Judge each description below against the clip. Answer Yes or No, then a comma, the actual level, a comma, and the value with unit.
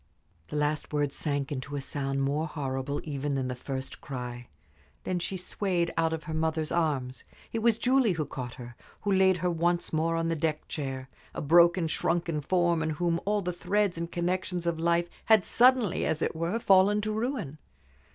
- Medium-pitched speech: Yes, medium, 165 Hz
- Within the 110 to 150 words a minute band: No, average, 190 wpm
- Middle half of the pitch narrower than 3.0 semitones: No, average, 3.9 semitones